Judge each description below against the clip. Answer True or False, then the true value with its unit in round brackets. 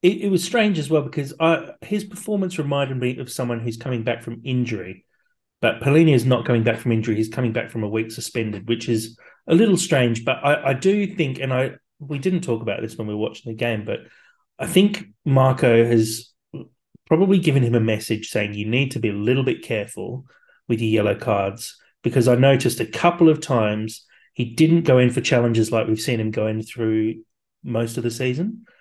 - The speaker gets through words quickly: True (215 wpm)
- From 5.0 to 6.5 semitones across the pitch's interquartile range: True (5.3 semitones)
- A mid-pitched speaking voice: False (125 Hz)